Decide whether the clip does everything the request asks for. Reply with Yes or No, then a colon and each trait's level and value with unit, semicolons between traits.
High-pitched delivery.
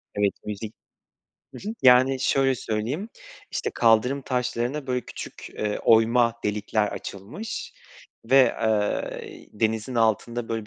No: low, 115 Hz